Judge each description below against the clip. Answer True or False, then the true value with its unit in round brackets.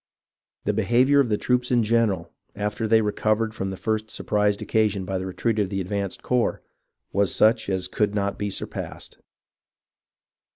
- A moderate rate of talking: True (170 wpm)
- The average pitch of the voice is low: True (105 Hz)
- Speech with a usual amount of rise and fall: False (2.2 semitones)